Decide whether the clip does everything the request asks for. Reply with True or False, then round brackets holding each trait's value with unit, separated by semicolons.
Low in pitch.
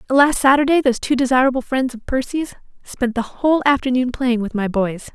False (255 Hz)